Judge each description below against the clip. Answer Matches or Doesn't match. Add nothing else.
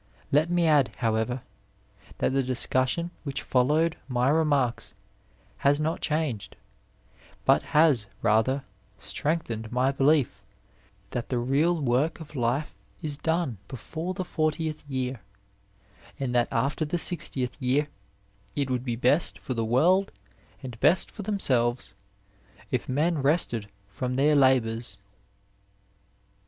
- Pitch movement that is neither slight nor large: Matches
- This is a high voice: Doesn't match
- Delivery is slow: Matches